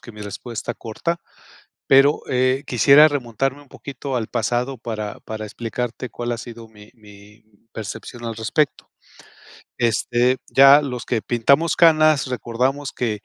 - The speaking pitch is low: Yes, low, 120 Hz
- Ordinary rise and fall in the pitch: Yes, average, 3.5 semitones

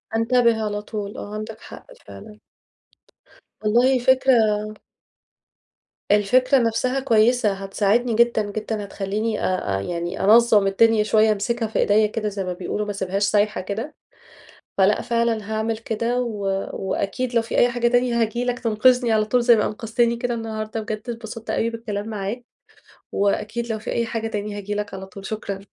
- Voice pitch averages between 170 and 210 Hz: No, high, 220 Hz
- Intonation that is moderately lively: No, narrow, 2.3 semitones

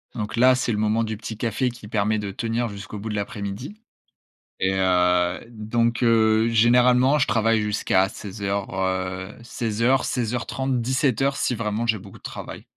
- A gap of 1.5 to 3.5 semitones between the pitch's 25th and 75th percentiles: Yes, average, 2.9 semitones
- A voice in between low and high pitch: No, low, 110 Hz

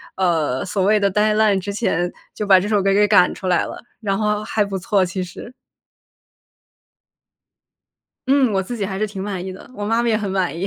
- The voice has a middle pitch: No, high, 200 Hz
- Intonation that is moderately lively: No, narrow, 2.2 semitones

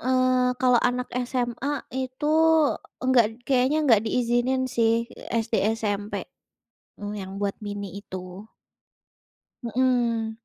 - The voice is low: No, high, 240 Hz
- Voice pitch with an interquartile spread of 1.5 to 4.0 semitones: Yes, average, 3.1 semitones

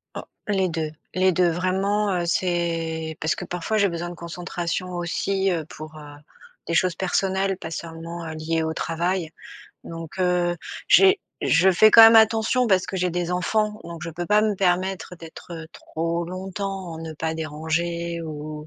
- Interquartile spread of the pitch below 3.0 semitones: Yes, narrow, 2.6 semitones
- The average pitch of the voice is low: No, medium, 175 Hz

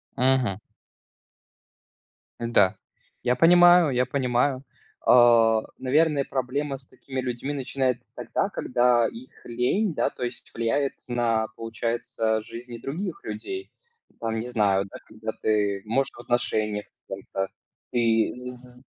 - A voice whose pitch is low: Yes, low, 120 Hz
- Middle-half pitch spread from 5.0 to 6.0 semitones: No, average, 2.8 semitones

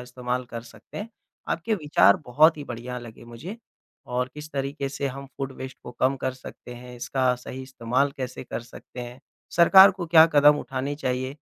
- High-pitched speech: No, low, 130 Hz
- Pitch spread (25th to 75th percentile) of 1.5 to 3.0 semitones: Yes, average, 2.7 semitones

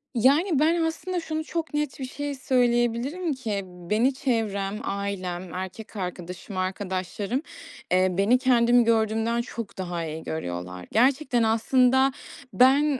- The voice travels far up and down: Yes, wide, 6.0 semitones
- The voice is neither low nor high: No, high, 230 Hz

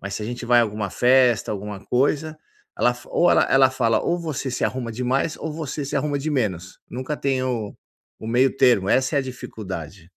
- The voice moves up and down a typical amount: Yes, average, 4.0 semitones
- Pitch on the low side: Yes, low, 125 Hz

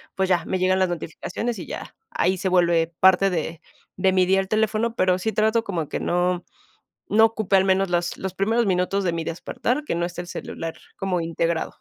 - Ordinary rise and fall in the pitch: No, narrow, 2.3 semitones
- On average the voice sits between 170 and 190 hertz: Yes, medium, 185 Hz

